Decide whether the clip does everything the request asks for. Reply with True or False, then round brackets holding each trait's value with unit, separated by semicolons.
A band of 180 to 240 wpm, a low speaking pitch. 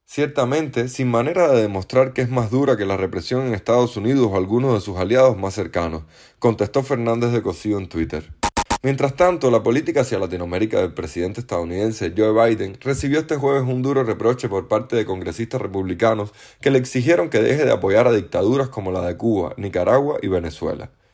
True (185 wpm; 115 Hz)